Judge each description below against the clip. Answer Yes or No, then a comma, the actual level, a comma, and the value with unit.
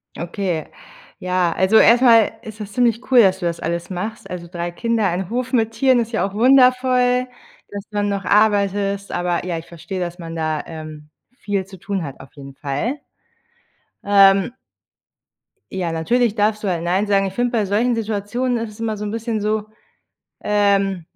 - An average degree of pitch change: Yes, average, 4.3 semitones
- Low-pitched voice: No, high, 200 Hz